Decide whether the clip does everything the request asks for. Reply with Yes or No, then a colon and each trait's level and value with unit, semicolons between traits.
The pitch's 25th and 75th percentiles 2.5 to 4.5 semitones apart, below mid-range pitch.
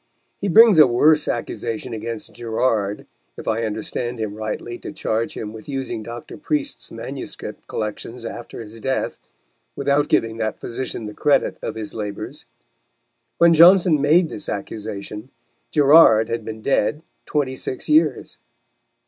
No: average, 5.0 semitones; low, 120 Hz